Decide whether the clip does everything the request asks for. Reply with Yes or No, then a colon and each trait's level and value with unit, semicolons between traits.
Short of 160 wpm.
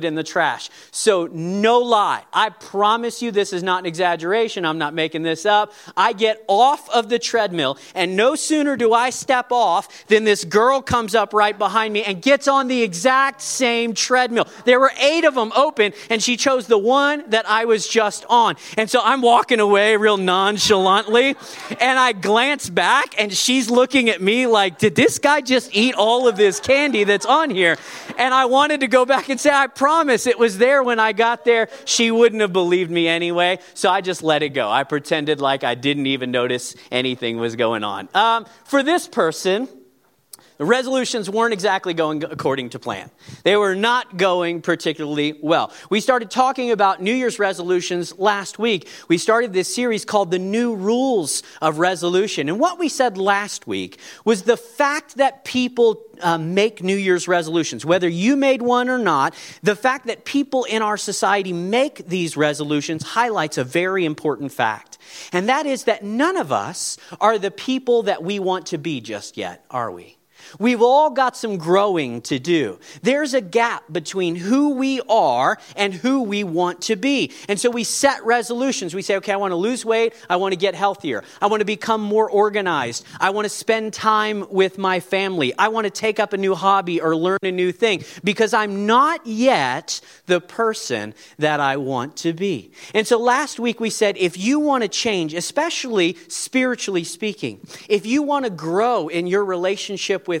No: average, 195 wpm